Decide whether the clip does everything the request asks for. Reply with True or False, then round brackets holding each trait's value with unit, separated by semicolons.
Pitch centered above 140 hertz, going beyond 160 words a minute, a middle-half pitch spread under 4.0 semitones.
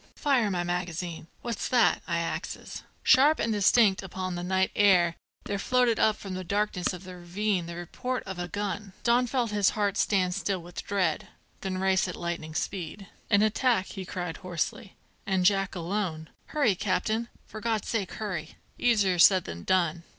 True (190 Hz; 175 wpm; 3.1 semitones)